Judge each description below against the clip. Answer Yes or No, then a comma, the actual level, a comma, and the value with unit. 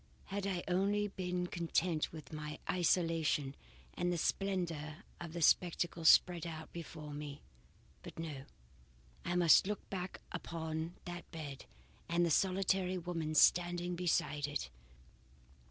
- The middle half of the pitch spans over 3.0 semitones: No, narrow, 2.4 semitones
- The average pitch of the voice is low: No, medium, 170 Hz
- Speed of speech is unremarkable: No, slow, 130 wpm